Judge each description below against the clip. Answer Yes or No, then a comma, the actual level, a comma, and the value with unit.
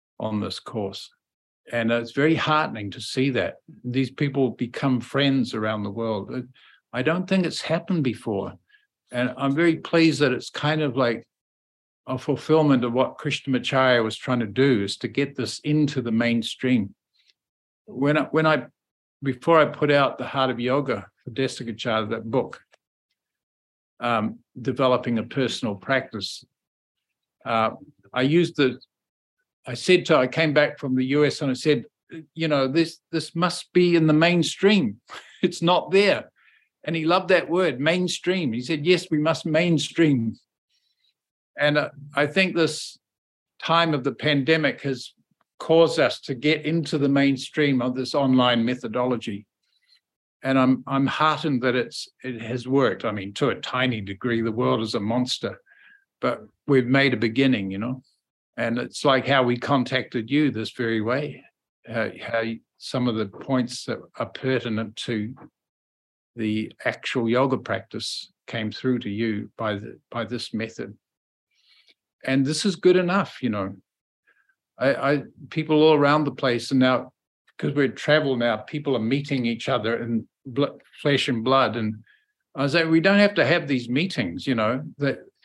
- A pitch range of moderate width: Yes, average, 4.5 semitones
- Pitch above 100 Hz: Yes, low, 135 Hz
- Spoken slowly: No, average, 165 wpm